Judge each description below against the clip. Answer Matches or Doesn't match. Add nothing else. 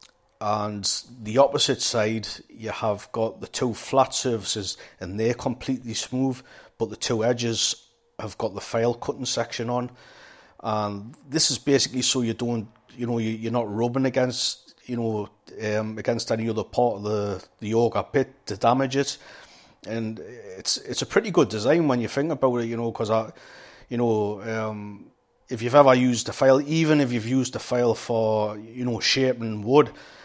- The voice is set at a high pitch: Doesn't match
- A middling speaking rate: Matches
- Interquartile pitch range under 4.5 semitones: Matches